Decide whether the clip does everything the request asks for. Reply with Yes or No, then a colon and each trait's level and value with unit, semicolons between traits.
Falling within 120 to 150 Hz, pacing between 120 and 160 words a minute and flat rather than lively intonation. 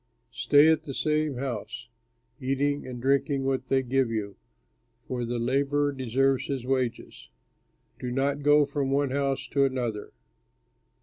Yes: low, 135 Hz; average, 140 wpm; narrow, 2.0 semitones